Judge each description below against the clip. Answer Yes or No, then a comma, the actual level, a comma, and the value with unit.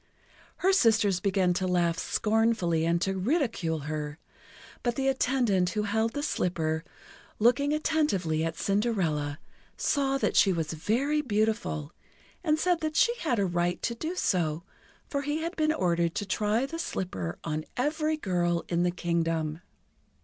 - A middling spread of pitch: No, wide, 8.0 semitones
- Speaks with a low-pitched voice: No, high, 200 Hz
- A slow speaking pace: No, average, 155 wpm